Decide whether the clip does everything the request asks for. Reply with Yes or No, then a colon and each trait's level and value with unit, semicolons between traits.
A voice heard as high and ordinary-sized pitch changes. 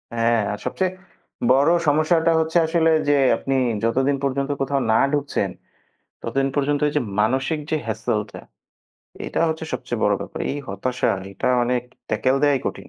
No: low, 135 Hz; average, 3.7 semitones